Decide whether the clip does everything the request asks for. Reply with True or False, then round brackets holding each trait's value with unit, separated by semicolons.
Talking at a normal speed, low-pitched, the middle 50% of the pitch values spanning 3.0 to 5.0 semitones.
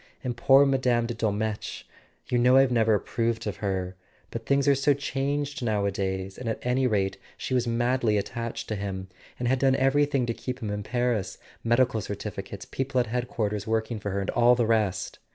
True (190 wpm; 115 Hz; 3.8 semitones)